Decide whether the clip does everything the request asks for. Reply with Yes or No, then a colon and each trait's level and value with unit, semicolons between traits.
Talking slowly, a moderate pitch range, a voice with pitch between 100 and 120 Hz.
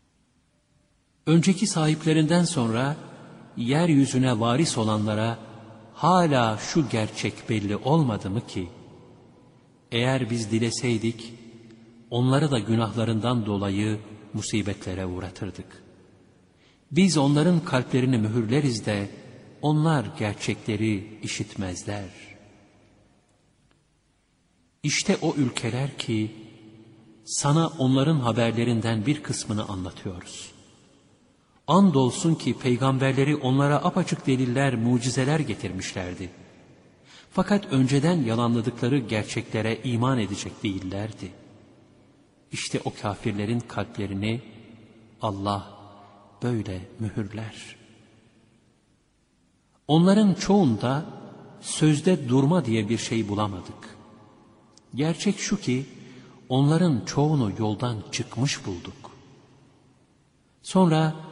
Yes: slow, 75 wpm; average, 4.6 semitones; low, 115 Hz